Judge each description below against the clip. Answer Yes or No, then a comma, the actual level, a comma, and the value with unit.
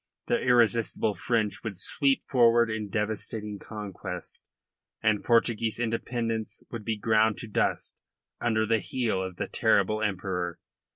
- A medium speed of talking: No, slow, 130 wpm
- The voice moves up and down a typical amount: No, narrow, 1.9 semitones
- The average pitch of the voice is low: Yes, low, 110 Hz